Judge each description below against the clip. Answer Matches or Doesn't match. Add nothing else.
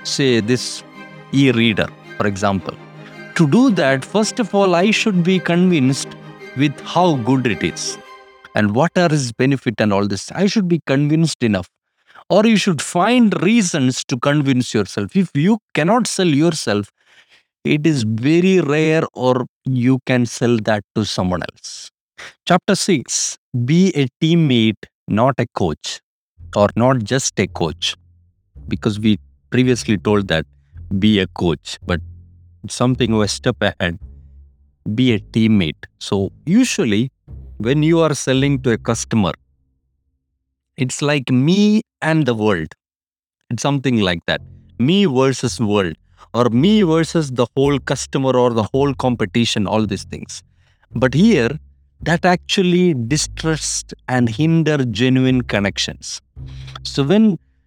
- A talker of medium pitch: Doesn't match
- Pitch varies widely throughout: Matches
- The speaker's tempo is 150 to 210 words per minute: Doesn't match